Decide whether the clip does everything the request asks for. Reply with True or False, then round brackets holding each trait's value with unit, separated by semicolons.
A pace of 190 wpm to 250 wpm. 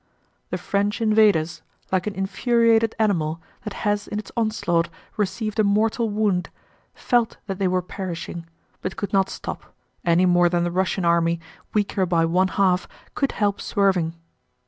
False (155 wpm)